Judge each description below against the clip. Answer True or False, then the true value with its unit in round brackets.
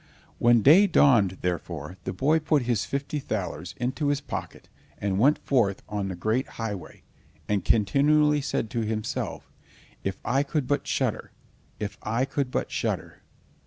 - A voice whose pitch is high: False (120 Hz)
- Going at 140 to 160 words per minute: True (155 wpm)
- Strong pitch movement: True (5.9 semitones)